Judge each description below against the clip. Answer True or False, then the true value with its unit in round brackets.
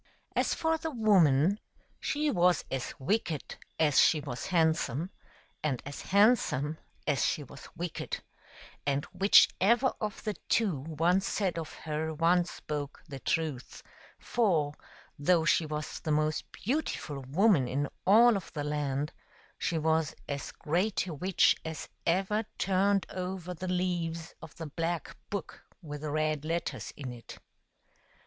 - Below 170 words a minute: True (140 wpm)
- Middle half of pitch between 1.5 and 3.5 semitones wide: False (4.4 semitones)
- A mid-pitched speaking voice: True (165 Hz)